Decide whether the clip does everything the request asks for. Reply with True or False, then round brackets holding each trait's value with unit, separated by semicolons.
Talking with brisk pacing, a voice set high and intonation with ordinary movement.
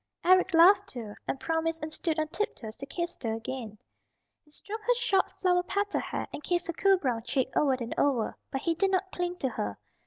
False (215 wpm; 330 Hz; 6.1 semitones)